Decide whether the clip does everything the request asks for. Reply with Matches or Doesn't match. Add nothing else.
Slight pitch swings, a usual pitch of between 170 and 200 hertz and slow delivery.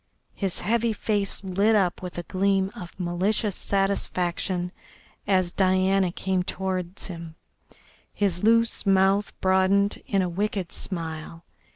Matches